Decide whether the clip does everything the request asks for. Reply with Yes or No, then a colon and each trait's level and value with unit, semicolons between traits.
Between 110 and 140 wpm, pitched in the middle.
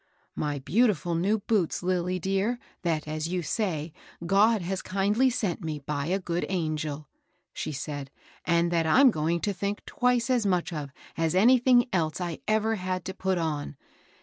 No: average, 175 wpm; medium, 180 Hz